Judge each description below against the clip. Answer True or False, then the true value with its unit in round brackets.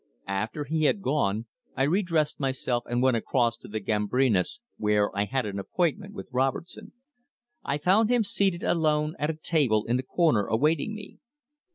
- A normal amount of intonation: False (6.6 semitones)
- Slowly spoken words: False (175 wpm)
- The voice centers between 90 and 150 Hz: True (135 Hz)